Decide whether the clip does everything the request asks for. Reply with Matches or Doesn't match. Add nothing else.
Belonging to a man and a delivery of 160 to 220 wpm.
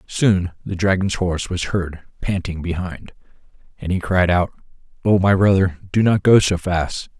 Matches